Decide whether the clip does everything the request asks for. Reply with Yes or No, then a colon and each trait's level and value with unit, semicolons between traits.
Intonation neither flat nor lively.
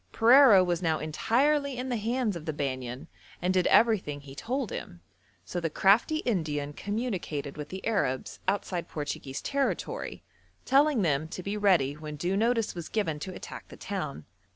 No: wide, 7.3 semitones